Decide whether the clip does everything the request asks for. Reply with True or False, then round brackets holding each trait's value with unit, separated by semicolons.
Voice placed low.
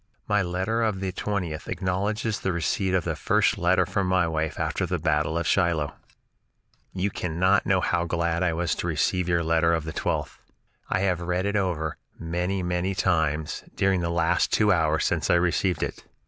True (90 Hz)